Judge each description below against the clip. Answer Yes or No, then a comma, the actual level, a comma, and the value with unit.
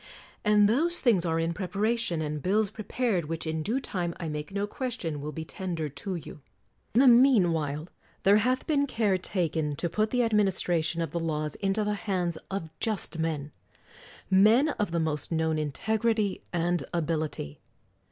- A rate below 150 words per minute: No, average, 175 wpm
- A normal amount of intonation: Yes, average, 5.0 semitones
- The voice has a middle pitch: Yes, medium, 180 Hz